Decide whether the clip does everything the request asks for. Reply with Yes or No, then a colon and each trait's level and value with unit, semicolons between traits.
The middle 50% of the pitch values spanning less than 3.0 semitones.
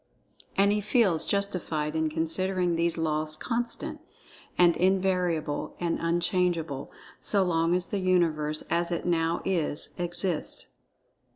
Yes: narrow, 2.4 semitones